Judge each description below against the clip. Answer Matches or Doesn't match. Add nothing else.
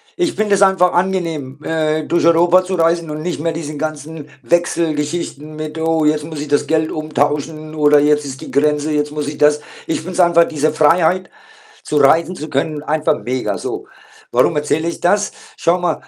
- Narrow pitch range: Matches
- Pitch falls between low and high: Matches